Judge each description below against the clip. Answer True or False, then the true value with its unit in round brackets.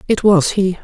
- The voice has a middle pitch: False (195 Hz)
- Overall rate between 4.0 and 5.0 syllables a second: True (4.6 syllables/s)